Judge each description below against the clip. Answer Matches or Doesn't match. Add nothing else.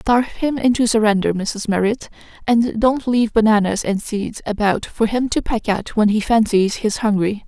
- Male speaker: Doesn't match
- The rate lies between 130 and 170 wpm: Doesn't match